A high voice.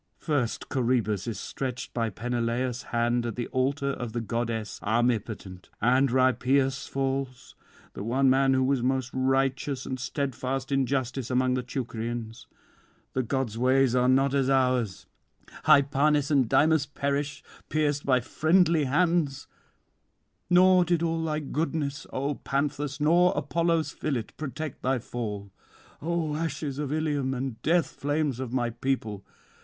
No: low, 135 Hz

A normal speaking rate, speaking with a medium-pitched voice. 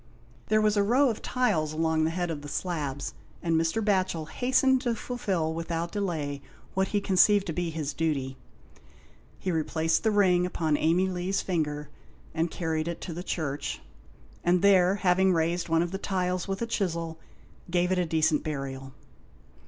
Yes: average, 170 wpm; medium, 175 Hz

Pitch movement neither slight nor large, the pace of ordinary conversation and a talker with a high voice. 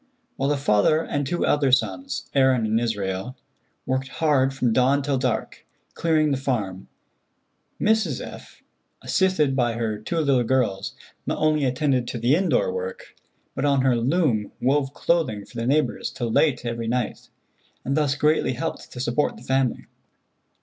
No: average, 4.0 semitones; average, 160 wpm; low, 135 Hz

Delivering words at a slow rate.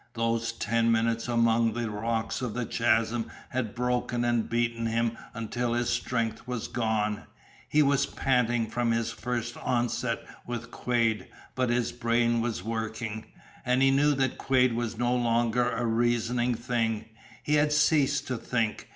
No: average, 155 wpm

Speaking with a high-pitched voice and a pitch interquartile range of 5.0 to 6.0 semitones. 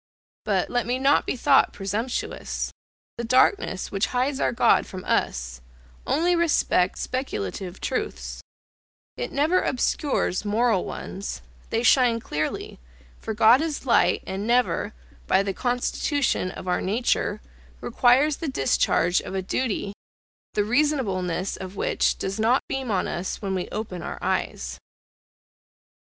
Yes: high, 225 Hz; wide, 5.5 semitones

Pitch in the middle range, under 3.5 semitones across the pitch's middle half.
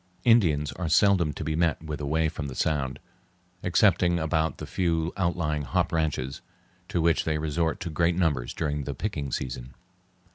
No: very low, 80 Hz; average, 2.7 semitones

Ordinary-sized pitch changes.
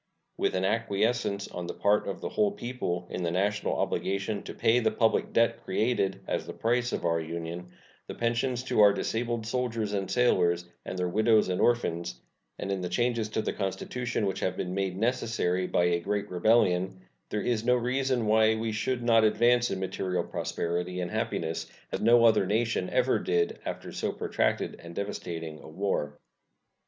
Yes: average, 4.4 semitones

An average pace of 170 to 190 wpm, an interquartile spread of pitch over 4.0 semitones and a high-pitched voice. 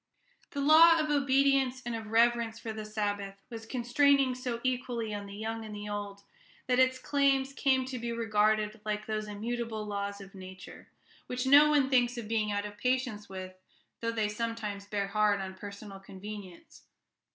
No: average, 175 wpm; average, 3.6 semitones; high, 225 Hz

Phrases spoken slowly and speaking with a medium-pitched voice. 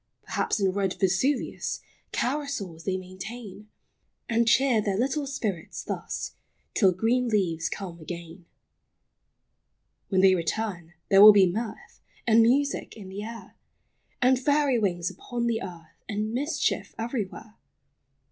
No: slow, 130 wpm; high, 210 Hz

